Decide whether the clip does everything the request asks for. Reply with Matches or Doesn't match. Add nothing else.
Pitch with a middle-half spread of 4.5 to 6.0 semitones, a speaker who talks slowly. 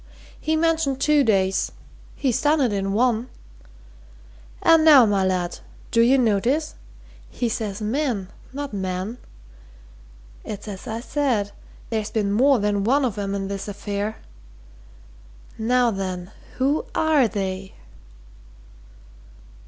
Matches